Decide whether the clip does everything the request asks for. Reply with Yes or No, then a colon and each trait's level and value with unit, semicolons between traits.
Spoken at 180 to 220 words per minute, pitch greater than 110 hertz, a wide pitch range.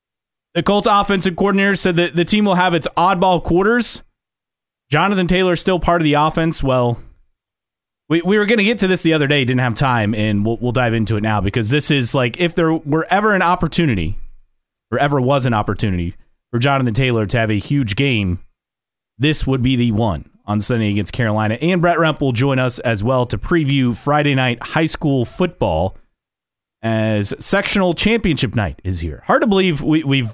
Yes: average, 200 wpm; low, 135 Hz; wide, 7.4 semitones